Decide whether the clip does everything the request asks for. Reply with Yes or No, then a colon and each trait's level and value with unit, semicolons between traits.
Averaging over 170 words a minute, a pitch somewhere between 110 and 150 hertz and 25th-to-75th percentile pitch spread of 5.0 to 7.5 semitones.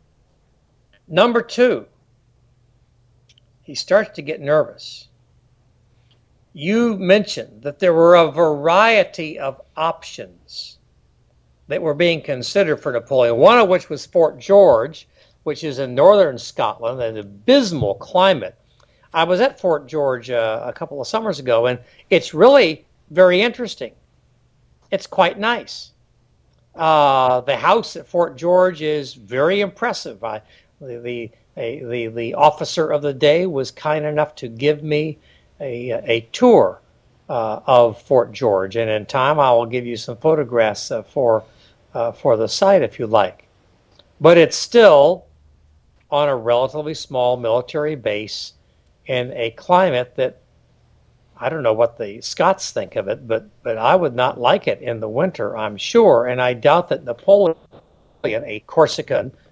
No: average, 145 wpm; low, 135 Hz; wide, 5.6 semitones